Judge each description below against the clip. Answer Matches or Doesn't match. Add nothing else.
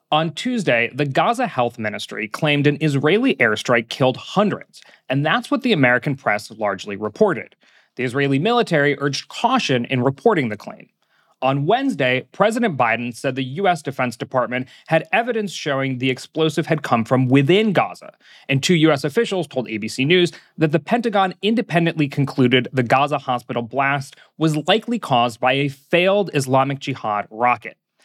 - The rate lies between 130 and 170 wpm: Matches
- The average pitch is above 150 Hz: Doesn't match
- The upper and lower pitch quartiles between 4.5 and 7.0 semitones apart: Matches